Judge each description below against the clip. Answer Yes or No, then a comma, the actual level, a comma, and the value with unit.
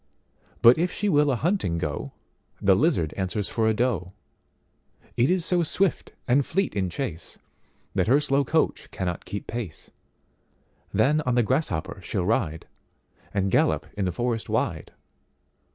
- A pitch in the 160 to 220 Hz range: No, low, 115 Hz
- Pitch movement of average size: No, wide, 7.4 semitones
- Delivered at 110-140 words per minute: Yes, slow, 135 wpm